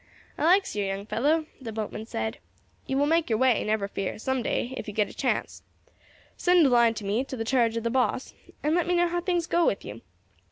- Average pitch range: No, wide, 6.9 semitones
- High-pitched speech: Yes, high, 245 Hz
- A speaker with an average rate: No, fast, 240 wpm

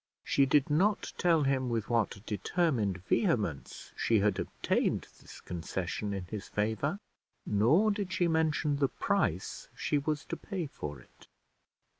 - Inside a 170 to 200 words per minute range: No, average, 145 wpm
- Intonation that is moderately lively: No, wide, 7.6 semitones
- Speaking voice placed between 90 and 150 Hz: Yes, low, 135 Hz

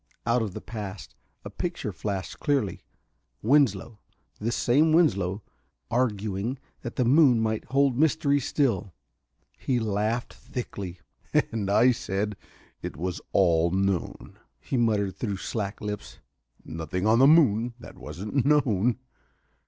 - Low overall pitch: Yes, low, 110 Hz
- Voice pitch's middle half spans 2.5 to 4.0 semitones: No, average, 4.5 semitones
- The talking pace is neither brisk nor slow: No, slow, 130 wpm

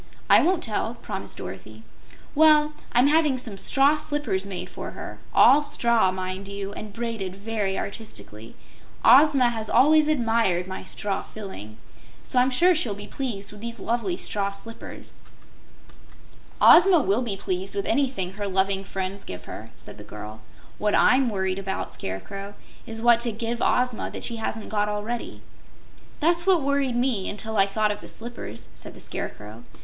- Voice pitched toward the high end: Yes, high, 215 Hz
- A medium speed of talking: Yes, average, 165 wpm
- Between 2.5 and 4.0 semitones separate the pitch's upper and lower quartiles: No, average, 4.6 semitones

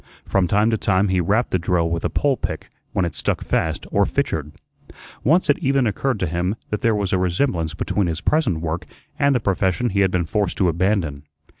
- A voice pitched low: Yes, very low, 95 Hz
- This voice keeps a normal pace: No, fast, 215 wpm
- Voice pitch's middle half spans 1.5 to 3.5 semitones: No, average, 4.2 semitones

